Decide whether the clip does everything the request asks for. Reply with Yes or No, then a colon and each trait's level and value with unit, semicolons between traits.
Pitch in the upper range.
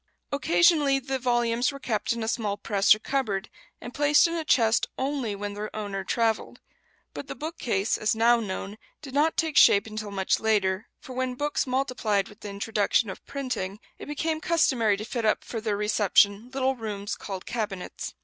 Yes: high, 225 Hz